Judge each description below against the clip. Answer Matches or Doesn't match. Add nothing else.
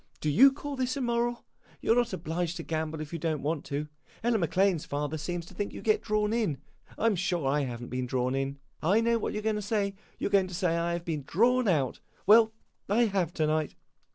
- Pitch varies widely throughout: Matches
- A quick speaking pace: Matches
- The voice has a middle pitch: Matches